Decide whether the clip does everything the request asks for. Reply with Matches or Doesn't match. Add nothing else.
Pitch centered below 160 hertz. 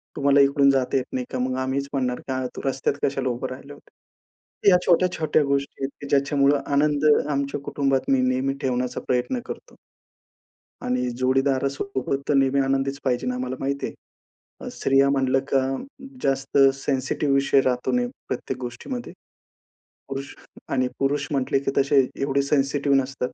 Matches